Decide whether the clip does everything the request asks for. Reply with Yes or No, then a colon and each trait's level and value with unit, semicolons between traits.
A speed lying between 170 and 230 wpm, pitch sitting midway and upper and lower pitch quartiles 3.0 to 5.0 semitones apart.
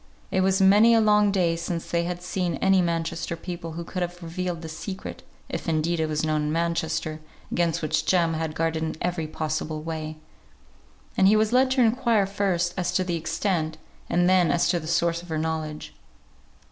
No: average, 195 wpm; medium, 170 Hz; narrow, 2.6 semitones